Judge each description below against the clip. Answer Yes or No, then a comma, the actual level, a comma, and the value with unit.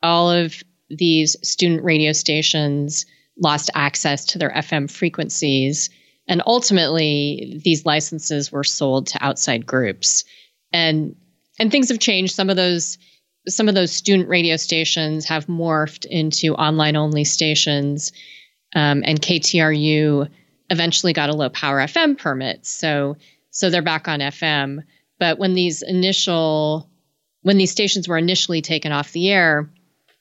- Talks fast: No, average, 140 wpm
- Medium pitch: Yes, medium, 160 Hz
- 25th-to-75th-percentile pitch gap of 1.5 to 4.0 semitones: Yes, average, 2.8 semitones